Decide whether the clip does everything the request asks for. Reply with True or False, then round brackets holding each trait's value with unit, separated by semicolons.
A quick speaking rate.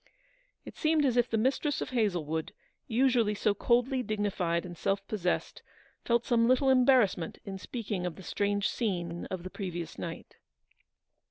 False (155 wpm)